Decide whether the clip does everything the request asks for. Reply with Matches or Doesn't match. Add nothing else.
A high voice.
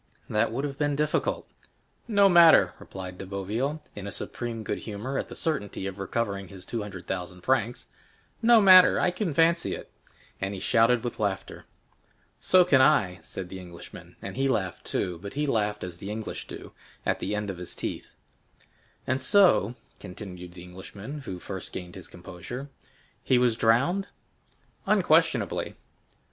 Doesn't match